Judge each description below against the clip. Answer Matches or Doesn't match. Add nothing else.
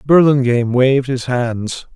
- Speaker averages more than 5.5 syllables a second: Doesn't match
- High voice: Doesn't match